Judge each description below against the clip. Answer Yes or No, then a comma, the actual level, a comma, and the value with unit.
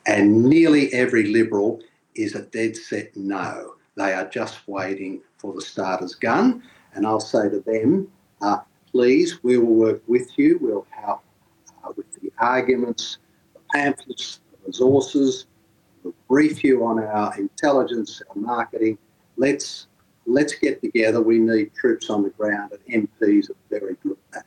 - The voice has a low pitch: Yes, low, 115 Hz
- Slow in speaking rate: No, average, 160 wpm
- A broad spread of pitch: Yes, wide, 7.3 semitones